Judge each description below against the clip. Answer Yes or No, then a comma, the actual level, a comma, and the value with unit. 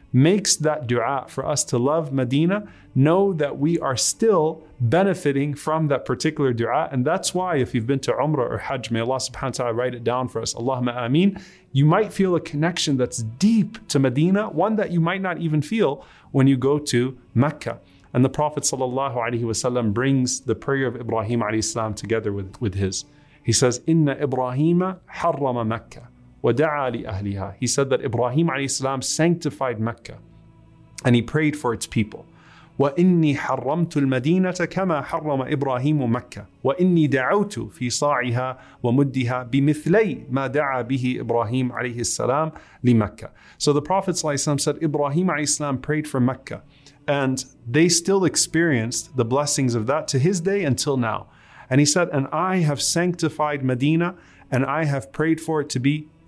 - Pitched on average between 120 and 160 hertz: Yes, medium, 140 Hz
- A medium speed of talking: Yes, average, 180 wpm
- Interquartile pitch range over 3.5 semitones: Yes, average, 4.2 semitones